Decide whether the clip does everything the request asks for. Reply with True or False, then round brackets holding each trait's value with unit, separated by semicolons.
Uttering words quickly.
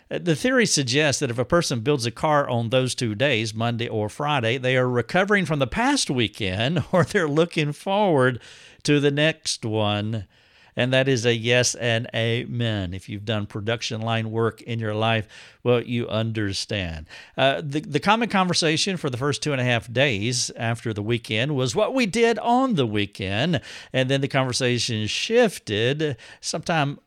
False (175 wpm)